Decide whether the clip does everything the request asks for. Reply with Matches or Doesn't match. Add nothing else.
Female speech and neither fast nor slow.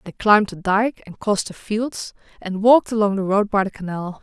Doesn't match